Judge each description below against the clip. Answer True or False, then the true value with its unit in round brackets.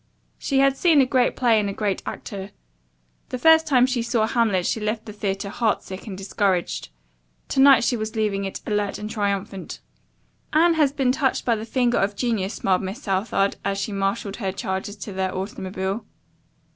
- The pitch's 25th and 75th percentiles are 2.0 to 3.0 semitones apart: False (3.9 semitones)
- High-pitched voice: True (210 Hz)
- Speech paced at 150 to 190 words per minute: True (185 wpm)